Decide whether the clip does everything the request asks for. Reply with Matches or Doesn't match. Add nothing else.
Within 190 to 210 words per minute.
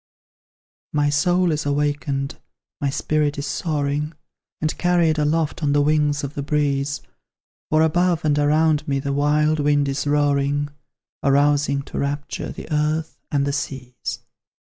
Doesn't match